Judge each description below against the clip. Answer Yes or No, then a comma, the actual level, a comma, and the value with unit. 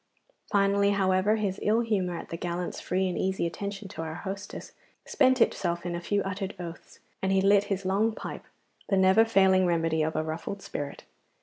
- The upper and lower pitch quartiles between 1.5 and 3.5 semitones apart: Yes, narrow, 2.5 semitones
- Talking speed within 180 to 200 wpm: Yes, average, 190 wpm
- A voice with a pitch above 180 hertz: Yes, high, 190 Hz